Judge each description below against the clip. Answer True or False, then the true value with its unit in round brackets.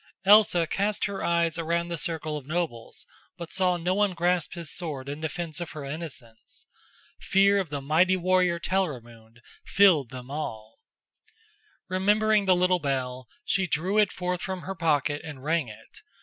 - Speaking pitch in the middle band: True (170 Hz)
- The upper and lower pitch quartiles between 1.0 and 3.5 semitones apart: False (4.2 semitones)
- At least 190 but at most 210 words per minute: False (165 wpm)